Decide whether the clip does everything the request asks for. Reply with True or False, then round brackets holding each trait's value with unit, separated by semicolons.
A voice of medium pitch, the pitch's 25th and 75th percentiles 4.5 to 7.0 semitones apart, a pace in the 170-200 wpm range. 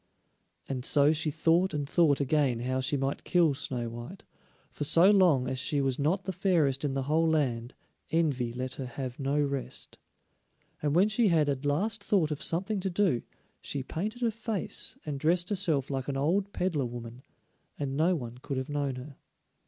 True (145 Hz; 4.8 semitones; 190 wpm)